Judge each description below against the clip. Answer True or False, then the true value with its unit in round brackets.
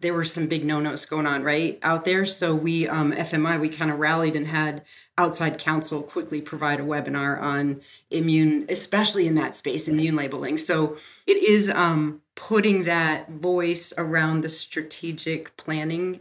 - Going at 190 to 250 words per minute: False (165 wpm)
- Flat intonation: True (1.8 semitones)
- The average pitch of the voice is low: False (160 Hz)